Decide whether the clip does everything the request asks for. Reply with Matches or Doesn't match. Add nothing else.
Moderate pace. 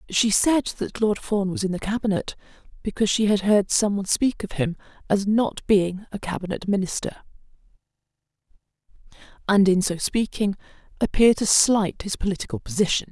Matches